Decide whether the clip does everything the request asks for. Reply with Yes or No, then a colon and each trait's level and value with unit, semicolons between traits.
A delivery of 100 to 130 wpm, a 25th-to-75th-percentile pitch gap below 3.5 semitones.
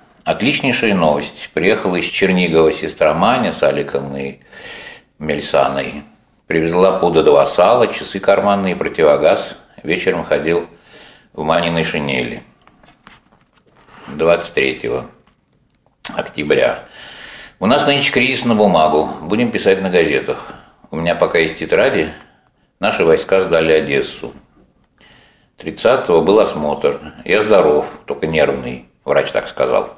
No: slow, 110 wpm; wide, 5.4 semitones